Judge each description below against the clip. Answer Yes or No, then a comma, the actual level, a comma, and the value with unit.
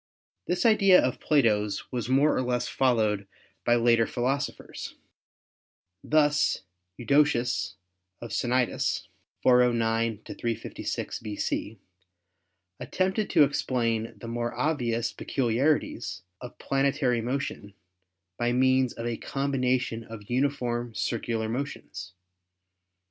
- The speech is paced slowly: Yes, slow, 105 wpm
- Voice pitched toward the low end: Yes, low, 120 Hz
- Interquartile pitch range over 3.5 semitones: No, average, 3.1 semitones